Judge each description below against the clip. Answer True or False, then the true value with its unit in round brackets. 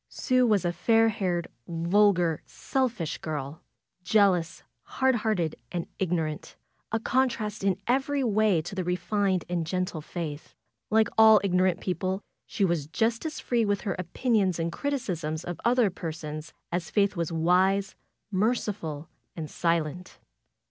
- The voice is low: False (185 Hz)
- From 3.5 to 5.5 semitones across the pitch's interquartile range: True (4.4 semitones)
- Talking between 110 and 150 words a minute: True (140 wpm)